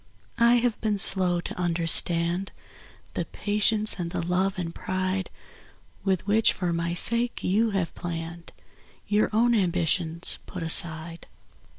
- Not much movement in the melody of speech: No, average, 3.6 semitones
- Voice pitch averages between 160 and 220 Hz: Yes, medium, 185 Hz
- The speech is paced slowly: Yes, slow, 125 wpm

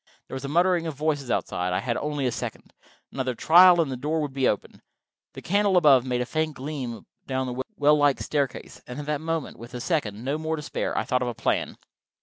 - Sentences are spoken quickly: Yes, fast, 230 wpm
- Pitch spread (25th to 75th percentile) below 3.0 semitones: No, average, 3.8 semitones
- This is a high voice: No, medium, 145 Hz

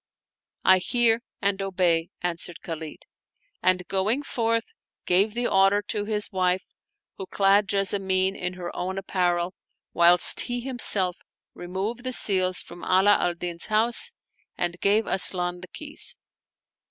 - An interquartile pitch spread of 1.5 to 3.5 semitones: Yes, average, 2.8 semitones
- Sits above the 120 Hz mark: Yes, high, 190 Hz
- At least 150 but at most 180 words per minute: No, average, 140 wpm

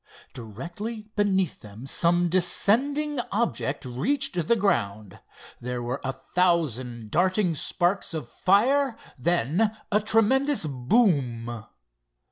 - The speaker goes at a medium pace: No, slow, 100 wpm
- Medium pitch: Yes, medium, 175 Hz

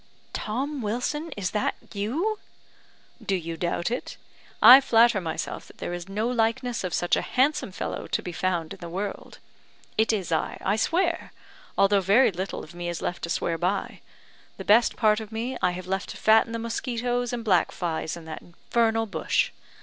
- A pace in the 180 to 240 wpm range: Yes, average, 190 wpm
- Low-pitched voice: No, high, 210 Hz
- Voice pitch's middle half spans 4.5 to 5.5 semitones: Yes, average, 5.1 semitones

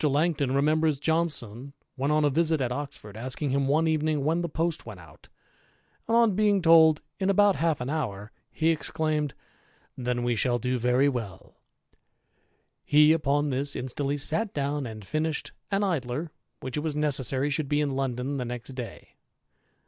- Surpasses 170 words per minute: Yes, average, 180 wpm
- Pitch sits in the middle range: Yes, medium, 145 Hz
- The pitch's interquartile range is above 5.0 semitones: No, average, 3.7 semitones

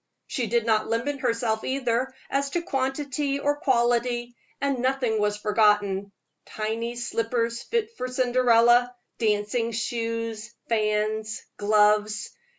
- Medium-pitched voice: No, high, 235 Hz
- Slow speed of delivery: Yes, slow, 115 wpm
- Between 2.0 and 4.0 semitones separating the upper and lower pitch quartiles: Yes, average, 2.8 semitones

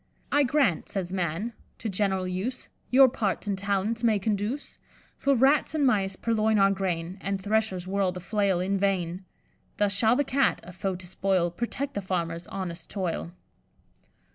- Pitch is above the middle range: Yes, high, 195 Hz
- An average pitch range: Yes, average, 3.3 semitones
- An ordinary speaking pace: Yes, average, 165 wpm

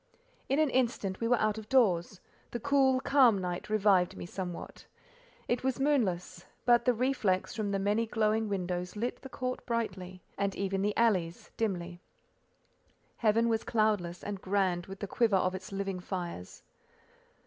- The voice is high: Yes, high, 205 Hz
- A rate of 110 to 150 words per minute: No, average, 160 wpm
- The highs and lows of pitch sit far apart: No, average, 4.1 semitones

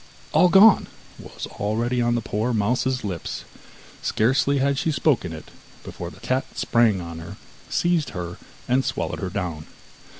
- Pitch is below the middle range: Yes, low, 120 Hz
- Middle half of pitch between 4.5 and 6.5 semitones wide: Yes, wide, 5.6 semitones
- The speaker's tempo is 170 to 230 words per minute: No, average, 155 wpm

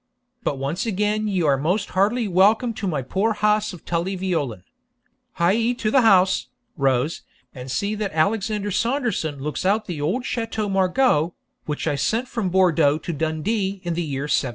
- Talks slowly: No, average, 175 wpm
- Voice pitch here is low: No, high, 190 Hz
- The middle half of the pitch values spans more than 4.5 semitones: Yes, wide, 5.4 semitones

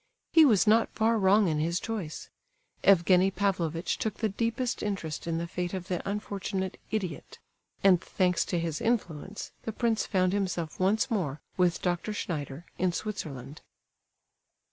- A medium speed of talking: Yes, average, 150 wpm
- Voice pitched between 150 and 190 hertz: Yes, medium, 185 Hz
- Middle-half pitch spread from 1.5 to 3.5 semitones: No, average, 3.9 semitones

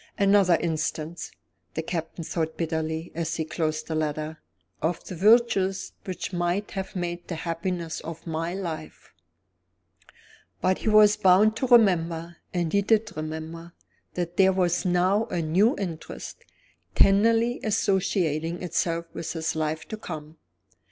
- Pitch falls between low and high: Yes, medium, 175 Hz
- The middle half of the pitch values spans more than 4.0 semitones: No, average, 3.2 semitones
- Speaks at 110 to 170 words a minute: Yes, average, 140 wpm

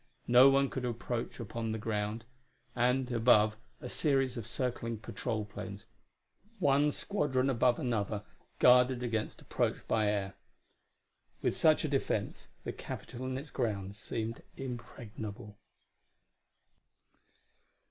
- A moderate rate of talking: No, slow, 115 wpm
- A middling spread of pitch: Yes, average, 3.0 semitones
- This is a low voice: Yes, low, 120 Hz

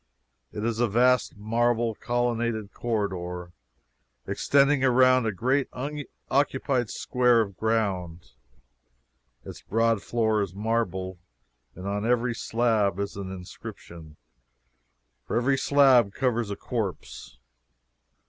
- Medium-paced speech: No, slow, 110 wpm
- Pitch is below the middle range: Yes, low, 115 Hz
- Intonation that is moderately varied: Yes, average, 3.6 semitones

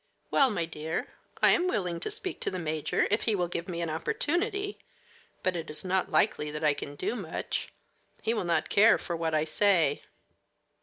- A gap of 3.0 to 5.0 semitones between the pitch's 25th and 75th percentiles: No, wide, 5.5 semitones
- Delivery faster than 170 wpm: Yes, average, 200 wpm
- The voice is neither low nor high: Yes, medium, 175 Hz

